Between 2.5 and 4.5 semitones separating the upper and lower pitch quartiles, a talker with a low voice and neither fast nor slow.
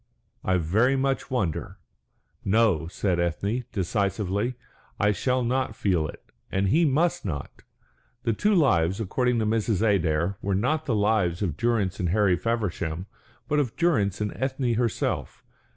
No: average, 5.1 semitones; low, 105 Hz; average, 150 wpm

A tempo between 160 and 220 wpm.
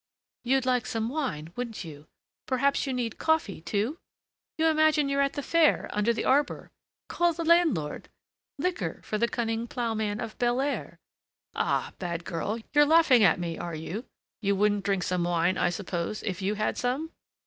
Yes: average, 170 wpm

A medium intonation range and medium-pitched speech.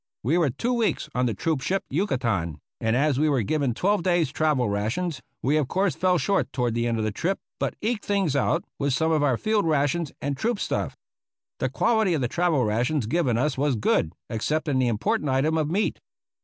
No: wide, 6.1 semitones; medium, 150 Hz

